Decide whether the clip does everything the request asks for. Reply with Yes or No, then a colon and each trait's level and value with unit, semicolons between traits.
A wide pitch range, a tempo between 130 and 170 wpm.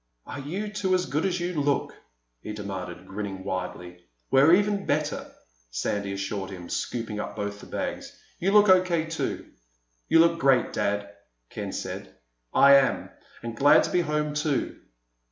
Yes: wide, 8.7 semitones; average, 160 wpm